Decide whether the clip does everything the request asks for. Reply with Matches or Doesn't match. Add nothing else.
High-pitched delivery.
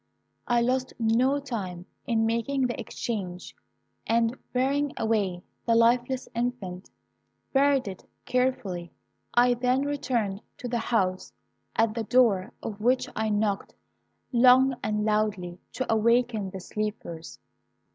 Matches